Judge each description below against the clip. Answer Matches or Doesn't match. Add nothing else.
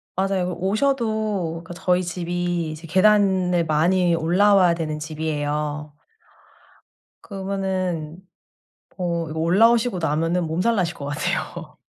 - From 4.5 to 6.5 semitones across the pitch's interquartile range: Doesn't match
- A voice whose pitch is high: Doesn't match